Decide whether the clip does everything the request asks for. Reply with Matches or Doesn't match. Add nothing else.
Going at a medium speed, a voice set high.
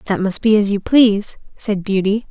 Doesn't match